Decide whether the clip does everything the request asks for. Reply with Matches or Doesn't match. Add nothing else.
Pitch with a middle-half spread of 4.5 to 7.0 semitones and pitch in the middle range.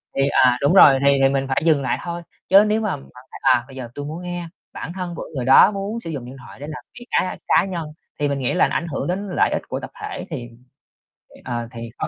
Matches